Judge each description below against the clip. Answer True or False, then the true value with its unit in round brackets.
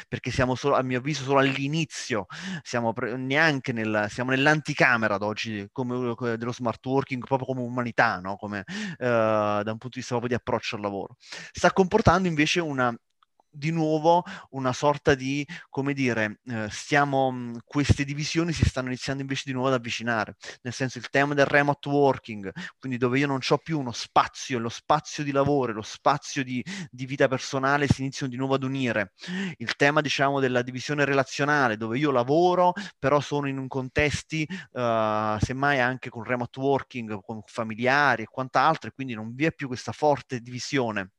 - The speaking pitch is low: True (130 Hz)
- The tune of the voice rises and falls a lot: False (3.2 semitones)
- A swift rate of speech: True (175 wpm)